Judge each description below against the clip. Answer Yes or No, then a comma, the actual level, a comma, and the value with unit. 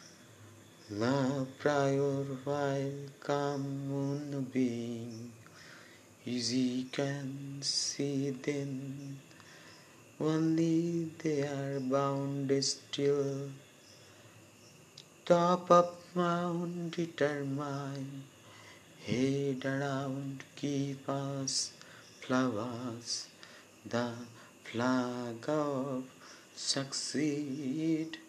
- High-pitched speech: No, medium, 140 Hz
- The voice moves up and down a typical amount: No, narrow, 2.0 semitones